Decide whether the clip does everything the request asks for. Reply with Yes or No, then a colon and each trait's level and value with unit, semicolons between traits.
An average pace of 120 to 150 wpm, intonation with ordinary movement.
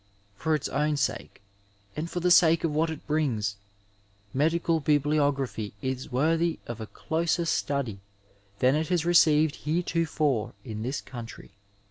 Yes: average, 145 wpm; average, 3.9 semitones